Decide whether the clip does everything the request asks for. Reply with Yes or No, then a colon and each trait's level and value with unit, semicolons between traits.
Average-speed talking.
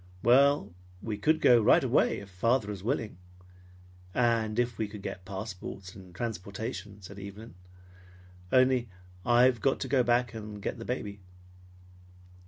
Yes: average, 145 wpm